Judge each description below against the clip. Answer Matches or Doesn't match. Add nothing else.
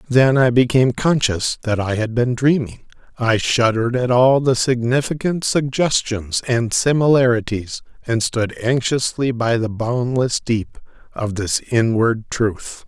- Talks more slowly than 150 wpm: Matches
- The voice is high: Doesn't match